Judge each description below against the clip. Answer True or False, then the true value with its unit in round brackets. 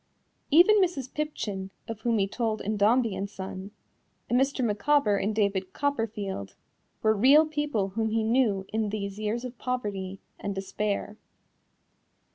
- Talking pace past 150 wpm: False (145 wpm)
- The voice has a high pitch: True (215 Hz)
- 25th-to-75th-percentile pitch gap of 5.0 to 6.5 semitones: False (4.1 semitones)